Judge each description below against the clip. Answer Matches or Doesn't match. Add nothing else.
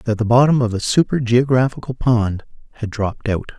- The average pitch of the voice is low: Matches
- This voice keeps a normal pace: Matches